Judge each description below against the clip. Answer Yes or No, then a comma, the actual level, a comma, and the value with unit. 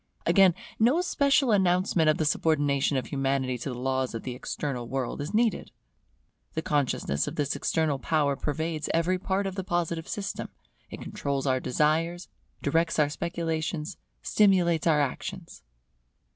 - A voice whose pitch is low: No, medium, 160 Hz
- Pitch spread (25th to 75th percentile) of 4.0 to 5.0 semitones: Yes, average, 4.3 semitones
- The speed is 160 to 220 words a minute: No, average, 150 wpm